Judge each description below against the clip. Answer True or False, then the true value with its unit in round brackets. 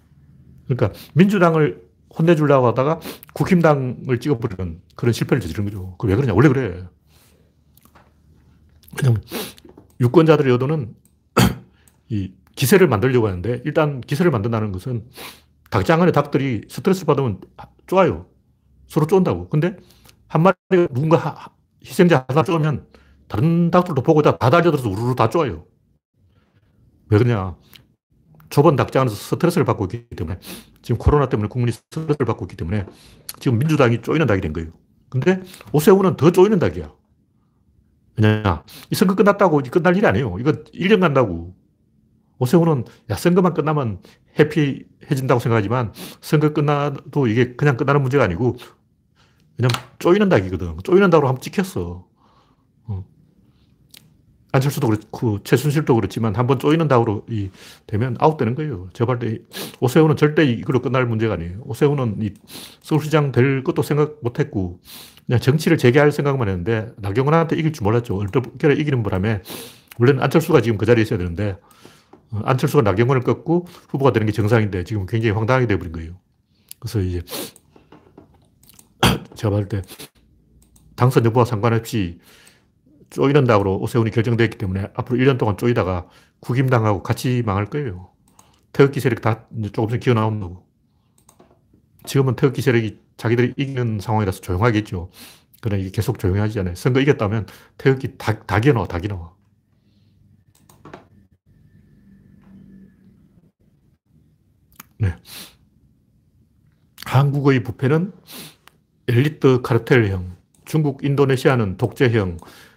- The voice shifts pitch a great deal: True (6.0 semitones)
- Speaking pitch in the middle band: False (125 Hz)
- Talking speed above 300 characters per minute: True (325 characters per minute)